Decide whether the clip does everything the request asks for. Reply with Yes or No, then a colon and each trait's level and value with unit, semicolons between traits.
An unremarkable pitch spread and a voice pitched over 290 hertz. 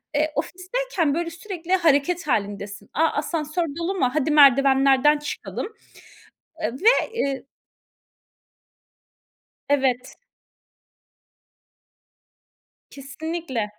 Yes: average, 4.0 semitones; very high, 300 Hz